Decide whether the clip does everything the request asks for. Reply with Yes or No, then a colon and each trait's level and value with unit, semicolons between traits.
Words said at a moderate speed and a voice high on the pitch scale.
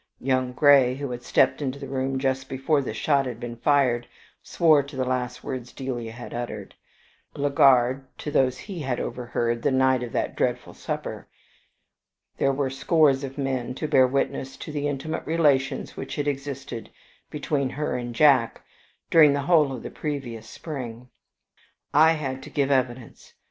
No: average, 170 wpm; low, 135 Hz